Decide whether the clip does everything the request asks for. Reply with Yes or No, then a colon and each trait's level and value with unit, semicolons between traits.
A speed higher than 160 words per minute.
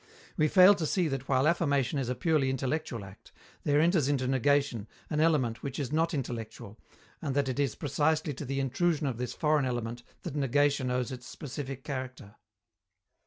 Yes: average, 180 wpm